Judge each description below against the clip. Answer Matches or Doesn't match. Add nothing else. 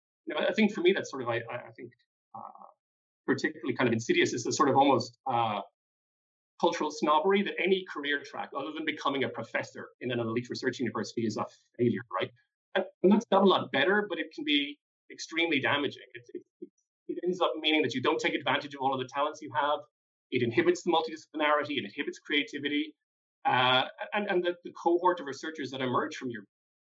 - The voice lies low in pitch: Doesn't match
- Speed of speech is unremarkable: Doesn't match